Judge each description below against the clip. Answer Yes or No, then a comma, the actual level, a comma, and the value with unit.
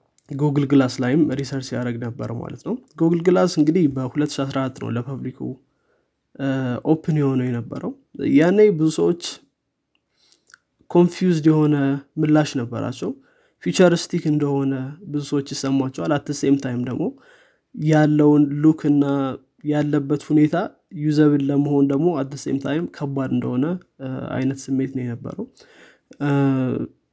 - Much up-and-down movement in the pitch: No, narrow, 2.5 semitones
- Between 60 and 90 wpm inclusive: No, fast, 110 wpm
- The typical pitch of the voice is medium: Yes, medium, 145 Hz